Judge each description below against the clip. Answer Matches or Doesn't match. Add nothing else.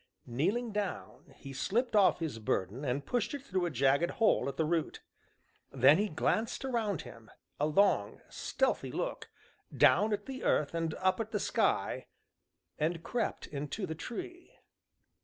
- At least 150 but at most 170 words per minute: Matches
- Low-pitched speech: Doesn't match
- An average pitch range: Doesn't match